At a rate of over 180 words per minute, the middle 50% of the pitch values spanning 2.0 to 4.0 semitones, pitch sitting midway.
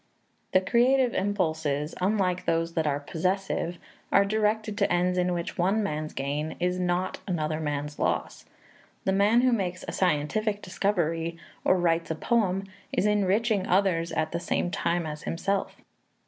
No: average, 155 wpm; average, 3.5 semitones; medium, 180 Hz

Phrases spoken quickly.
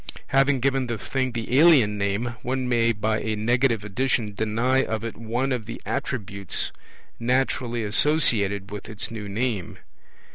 No: average, 150 wpm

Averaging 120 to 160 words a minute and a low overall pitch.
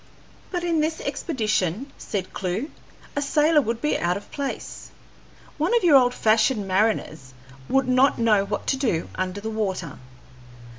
No: average, 155 wpm; high, 230 Hz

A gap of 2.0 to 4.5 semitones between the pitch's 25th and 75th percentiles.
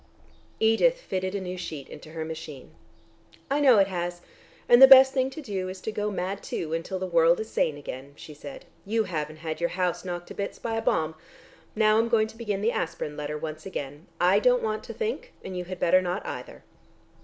No: wide, 5.4 semitones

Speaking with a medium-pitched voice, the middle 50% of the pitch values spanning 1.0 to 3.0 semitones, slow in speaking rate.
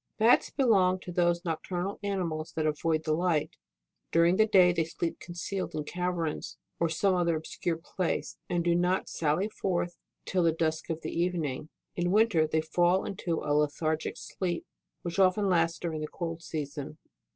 No: medium, 170 Hz; narrow, 2.4 semitones; average, 175 wpm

